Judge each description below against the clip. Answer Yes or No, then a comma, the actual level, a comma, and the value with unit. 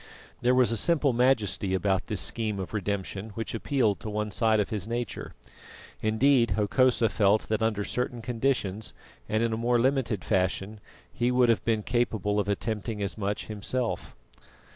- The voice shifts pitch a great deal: No, average, 2.8 semitones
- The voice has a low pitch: Yes, low, 110 Hz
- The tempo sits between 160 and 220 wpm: Yes, average, 165 wpm